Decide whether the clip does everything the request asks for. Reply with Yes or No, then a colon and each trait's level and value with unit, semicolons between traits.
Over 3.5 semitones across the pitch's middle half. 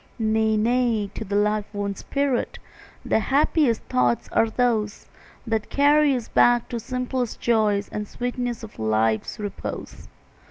No: average, 3.0 semitones